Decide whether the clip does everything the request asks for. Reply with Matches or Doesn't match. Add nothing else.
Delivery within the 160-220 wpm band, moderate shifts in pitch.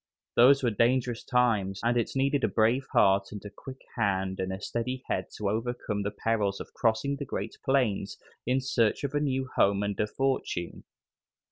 Matches